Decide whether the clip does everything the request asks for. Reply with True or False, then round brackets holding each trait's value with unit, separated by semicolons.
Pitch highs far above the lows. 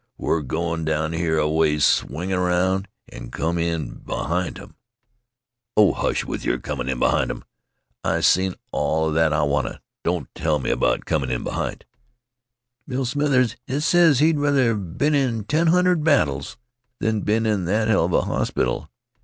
True (7.8 semitones)